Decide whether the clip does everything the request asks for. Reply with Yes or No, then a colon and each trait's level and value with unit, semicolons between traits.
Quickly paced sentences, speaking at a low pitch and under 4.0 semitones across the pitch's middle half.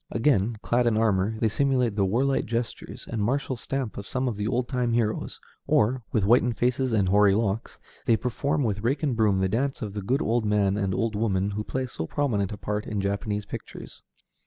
Yes: fast, 210 wpm; low, 110 Hz; average, 3.4 semitones